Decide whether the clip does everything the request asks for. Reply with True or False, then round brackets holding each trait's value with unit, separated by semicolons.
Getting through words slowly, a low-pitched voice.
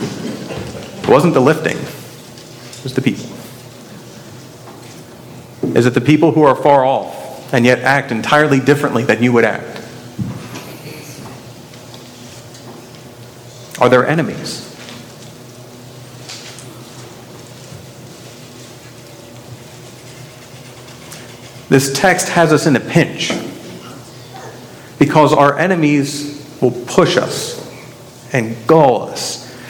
True (90 wpm; 125 Hz)